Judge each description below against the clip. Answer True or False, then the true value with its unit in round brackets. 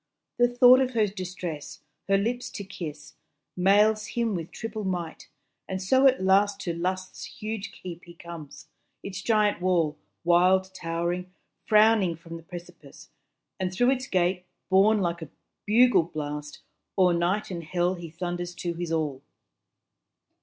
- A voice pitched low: False (185 Hz)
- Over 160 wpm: False (150 wpm)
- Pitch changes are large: False (3.5 semitones)